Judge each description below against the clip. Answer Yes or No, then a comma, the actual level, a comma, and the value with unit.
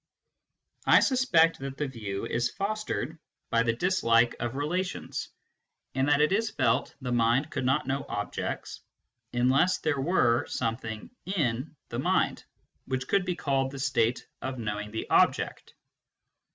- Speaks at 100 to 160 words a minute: Yes, average, 145 wpm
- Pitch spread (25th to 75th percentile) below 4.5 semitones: No, average, 5.3 semitones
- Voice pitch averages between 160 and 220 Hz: No, low, 135 Hz